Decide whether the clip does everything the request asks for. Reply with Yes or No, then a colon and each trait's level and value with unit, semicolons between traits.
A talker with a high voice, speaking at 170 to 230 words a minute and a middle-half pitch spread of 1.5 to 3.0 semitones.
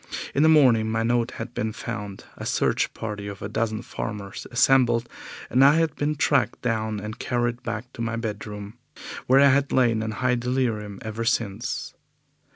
No: low, 115 Hz; average, 175 wpm; narrow, 2.6 semitones